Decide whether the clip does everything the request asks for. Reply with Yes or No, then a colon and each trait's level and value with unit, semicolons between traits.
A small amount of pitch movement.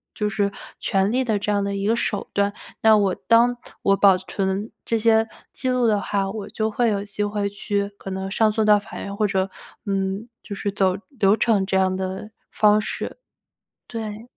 Yes: narrow, 1.9 semitones